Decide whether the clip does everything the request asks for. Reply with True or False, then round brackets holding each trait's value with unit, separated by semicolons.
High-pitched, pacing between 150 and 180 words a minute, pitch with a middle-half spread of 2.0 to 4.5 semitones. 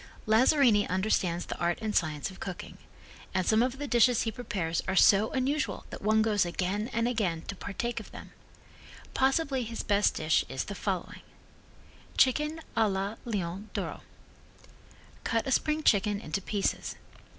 True (210 Hz; 160 wpm; 4.2 semitones)